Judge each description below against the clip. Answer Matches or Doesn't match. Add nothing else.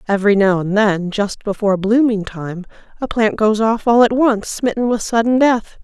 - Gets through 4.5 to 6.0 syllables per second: Matches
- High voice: Matches